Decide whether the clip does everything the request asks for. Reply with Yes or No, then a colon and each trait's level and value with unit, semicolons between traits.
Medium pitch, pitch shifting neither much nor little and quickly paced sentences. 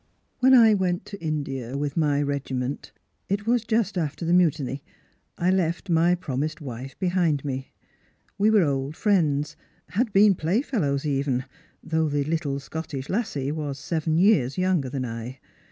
No: medium, 155 Hz; average, 4.8 semitones; average, 160 wpm